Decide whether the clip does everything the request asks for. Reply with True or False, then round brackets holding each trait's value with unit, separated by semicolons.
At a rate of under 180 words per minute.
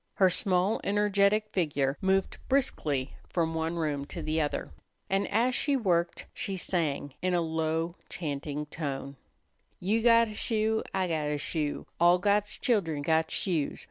True (155 wpm)